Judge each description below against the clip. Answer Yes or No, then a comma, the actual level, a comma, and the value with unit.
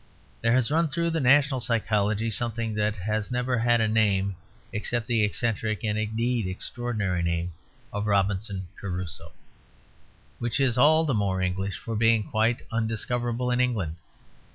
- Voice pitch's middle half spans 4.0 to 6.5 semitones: No, average, 3.1 semitones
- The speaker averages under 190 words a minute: Yes, average, 150 wpm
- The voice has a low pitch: Yes, low, 110 Hz